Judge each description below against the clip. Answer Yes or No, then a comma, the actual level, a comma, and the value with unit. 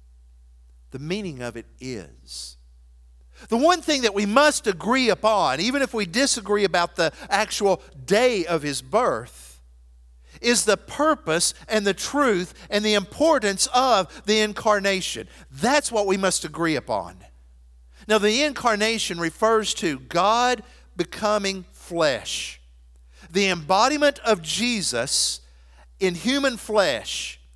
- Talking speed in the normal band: No, slow, 125 wpm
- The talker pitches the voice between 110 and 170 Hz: No, high, 190 Hz